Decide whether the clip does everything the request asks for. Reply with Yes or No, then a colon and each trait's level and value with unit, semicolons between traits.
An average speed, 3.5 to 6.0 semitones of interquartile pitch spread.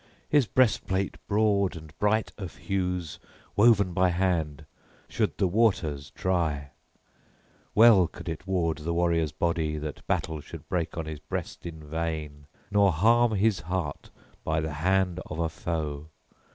Yes: average, 145 wpm; average, 3.8 semitones